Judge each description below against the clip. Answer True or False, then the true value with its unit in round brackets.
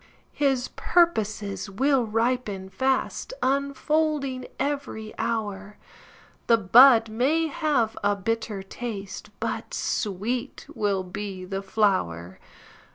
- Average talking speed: False (85 wpm)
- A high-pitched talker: True (225 Hz)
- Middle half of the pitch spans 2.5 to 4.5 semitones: False (5.1 semitones)